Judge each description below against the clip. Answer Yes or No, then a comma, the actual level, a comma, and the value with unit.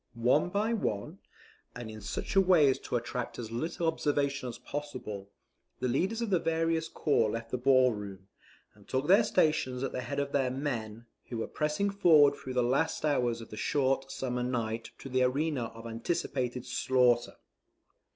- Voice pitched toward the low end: Yes, low, 130 Hz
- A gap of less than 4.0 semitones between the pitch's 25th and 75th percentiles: No, average, 4.3 semitones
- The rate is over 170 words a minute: Yes, average, 180 wpm